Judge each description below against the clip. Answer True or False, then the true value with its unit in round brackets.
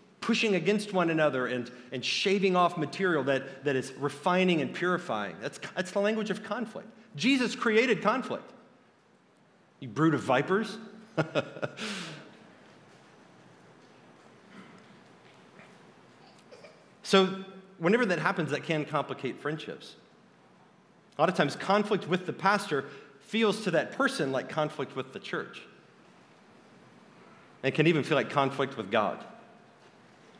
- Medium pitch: True (180 Hz)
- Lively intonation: True (6.3 semitones)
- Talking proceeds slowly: True (120 wpm)